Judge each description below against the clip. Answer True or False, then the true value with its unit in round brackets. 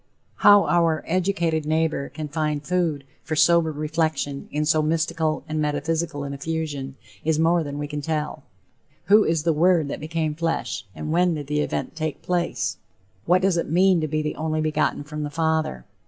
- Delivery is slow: False (185 wpm)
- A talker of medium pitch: True (155 Hz)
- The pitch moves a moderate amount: False (1.9 semitones)